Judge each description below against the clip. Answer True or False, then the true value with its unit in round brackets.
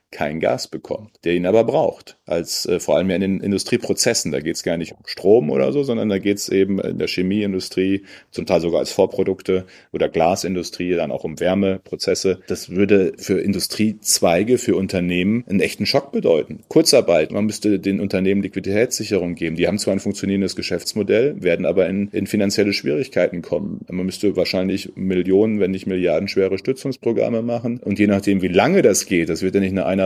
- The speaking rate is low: False (190 wpm)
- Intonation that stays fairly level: True (1.5 semitones)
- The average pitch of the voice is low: True (95 Hz)